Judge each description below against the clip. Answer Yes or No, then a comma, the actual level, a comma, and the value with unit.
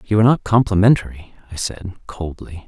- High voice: No, low, 100 Hz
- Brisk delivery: No, average, 155 wpm